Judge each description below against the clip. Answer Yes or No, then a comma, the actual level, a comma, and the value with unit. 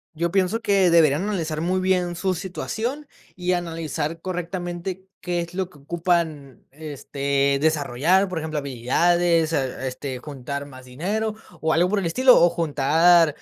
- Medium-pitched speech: Yes, medium, 170 Hz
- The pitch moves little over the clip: No, average, 3.8 semitones